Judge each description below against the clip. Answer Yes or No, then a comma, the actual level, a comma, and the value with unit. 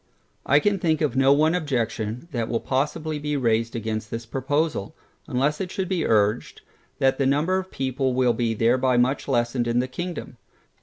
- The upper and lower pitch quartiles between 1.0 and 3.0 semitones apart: No, average, 4.3 semitones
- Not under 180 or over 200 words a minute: Yes, average, 185 wpm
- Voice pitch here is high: No, low, 130 Hz